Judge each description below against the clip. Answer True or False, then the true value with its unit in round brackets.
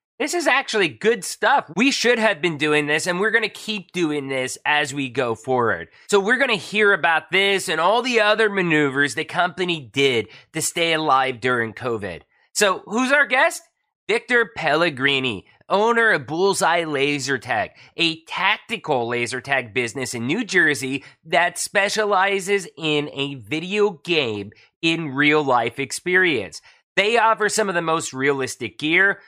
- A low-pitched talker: False (165 Hz)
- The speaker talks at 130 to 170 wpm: True (160 wpm)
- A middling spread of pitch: False (6.8 semitones)